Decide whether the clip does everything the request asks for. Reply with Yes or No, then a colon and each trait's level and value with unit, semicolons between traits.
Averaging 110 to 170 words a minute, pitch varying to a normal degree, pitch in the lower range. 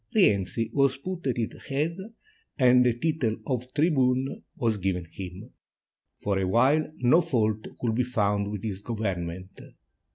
Yes: average, 150 wpm; average, 4.8 semitones; low, 115 Hz